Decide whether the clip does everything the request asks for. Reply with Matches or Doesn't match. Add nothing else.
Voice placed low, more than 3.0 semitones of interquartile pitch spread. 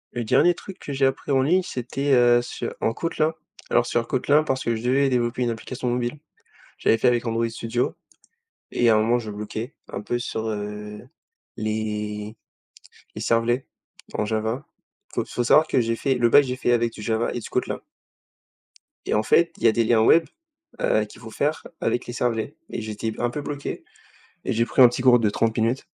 Doesn't match